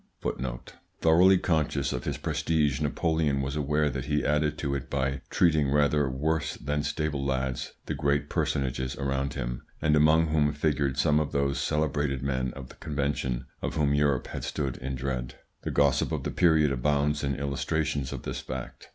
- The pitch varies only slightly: Yes, narrow, 2.0 semitones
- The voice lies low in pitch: Yes, very low, 70 Hz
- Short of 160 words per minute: No, average, 175 wpm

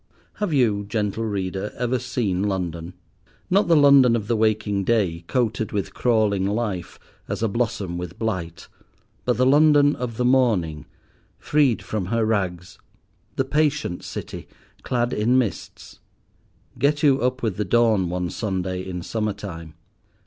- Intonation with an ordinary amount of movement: Yes, average, 5.0 semitones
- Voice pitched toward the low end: Yes, low, 110 Hz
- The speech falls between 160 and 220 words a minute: No, average, 145 wpm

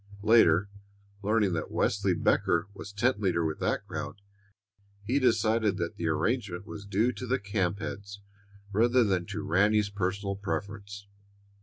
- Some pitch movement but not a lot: No, narrow, 2.3 semitones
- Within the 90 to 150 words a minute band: Yes, average, 145 wpm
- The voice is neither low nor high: No, low, 100 Hz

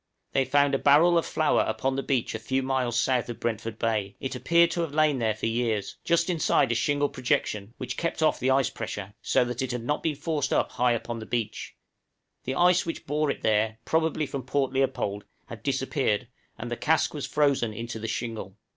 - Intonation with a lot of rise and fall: No, average, 4.3 semitones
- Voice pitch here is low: Yes, low, 130 Hz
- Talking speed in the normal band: No, fast, 215 wpm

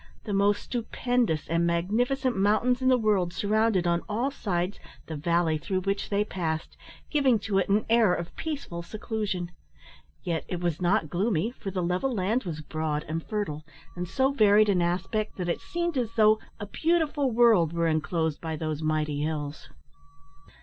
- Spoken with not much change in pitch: No, average, 4.8 semitones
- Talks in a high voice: Yes, high, 195 Hz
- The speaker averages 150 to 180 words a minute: Yes, average, 170 wpm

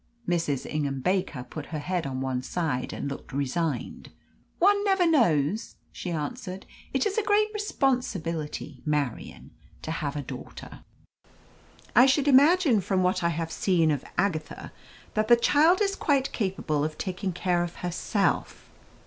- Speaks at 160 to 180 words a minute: No, average, 150 wpm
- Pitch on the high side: No, medium, 180 Hz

